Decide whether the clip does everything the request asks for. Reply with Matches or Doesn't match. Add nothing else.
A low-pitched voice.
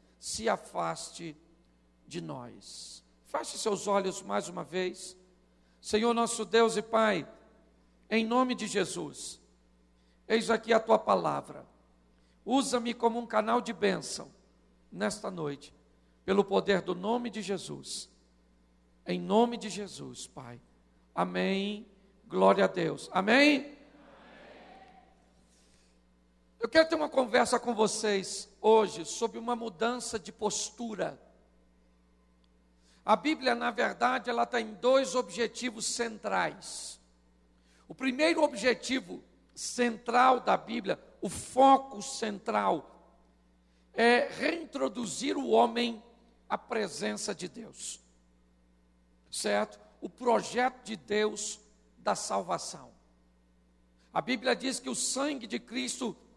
Doesn't match